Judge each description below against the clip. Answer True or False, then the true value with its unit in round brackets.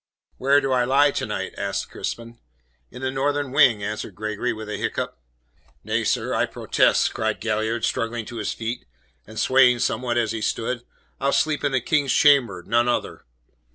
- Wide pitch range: False (3.5 semitones)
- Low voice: True (120 Hz)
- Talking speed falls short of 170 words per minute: False (180 wpm)